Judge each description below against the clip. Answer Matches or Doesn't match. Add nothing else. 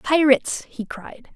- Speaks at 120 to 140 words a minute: Matches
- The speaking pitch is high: Matches